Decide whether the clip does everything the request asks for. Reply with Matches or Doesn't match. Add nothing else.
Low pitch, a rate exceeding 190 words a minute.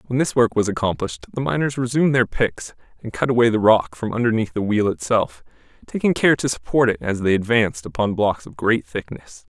Matches